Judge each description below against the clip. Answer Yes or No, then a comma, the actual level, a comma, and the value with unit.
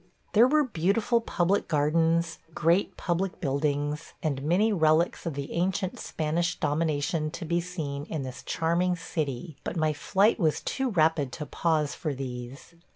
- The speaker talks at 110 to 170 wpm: Yes, average, 155 wpm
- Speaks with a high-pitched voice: No, medium, 165 Hz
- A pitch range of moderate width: Yes, average, 3.3 semitones